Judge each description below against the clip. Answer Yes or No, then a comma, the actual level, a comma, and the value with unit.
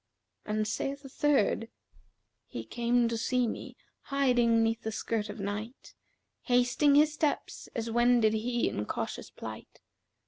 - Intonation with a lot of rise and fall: No, narrow, 2.5 semitones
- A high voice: Yes, high, 235 Hz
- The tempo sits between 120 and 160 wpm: Yes, average, 150 wpm